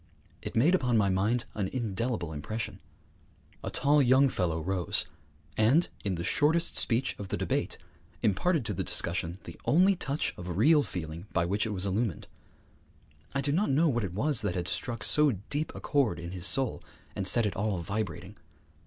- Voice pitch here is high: No, low, 110 Hz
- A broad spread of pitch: Yes, wide, 6.8 semitones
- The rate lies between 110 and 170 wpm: No, average, 185 wpm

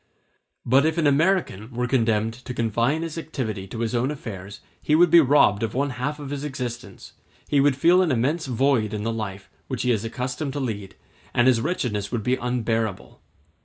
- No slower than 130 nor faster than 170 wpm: No, average, 200 wpm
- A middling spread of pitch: Yes, average, 4.3 semitones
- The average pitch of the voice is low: Yes, low, 125 Hz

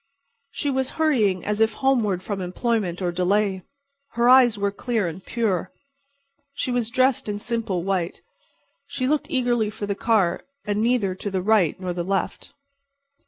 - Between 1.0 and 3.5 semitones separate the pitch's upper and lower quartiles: No, average, 4.2 semitones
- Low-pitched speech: No, high, 210 Hz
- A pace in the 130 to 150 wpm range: No, average, 165 wpm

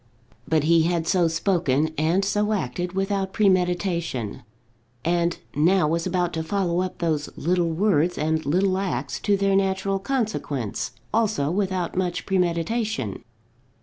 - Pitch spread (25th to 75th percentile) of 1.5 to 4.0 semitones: Yes, average, 3.3 semitones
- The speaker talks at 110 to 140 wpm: Yes, slow, 135 wpm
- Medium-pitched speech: Yes, medium, 175 Hz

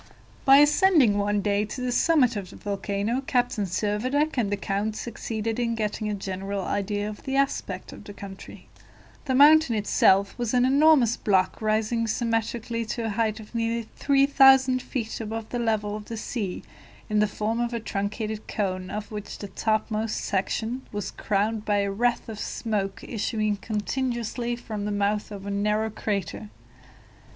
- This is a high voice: Yes, high, 215 Hz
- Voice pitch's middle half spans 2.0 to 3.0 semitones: Yes, average, 2.7 semitones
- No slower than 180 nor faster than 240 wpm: No, average, 170 wpm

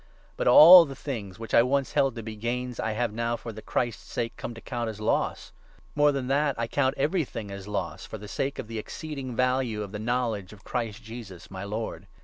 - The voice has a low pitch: Yes, low, 115 Hz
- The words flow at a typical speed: No, fast, 235 wpm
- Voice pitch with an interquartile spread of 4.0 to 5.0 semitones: No, average, 3.5 semitones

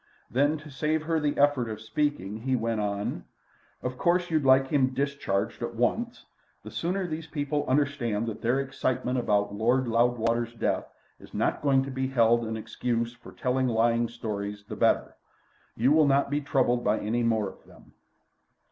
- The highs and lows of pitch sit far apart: No, average, 3.8 semitones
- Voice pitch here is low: Yes, low, 125 Hz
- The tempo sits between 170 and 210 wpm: Yes, average, 175 wpm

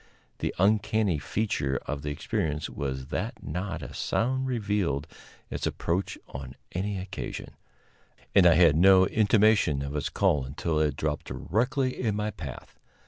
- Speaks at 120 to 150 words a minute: Yes, average, 145 wpm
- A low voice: Yes, very low, 90 Hz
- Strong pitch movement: Yes, wide, 6.2 semitones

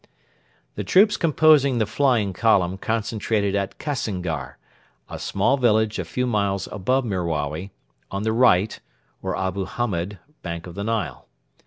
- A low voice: Yes, low, 105 Hz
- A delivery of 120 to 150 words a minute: Yes, average, 140 wpm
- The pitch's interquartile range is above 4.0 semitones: Yes, average, 4.6 semitones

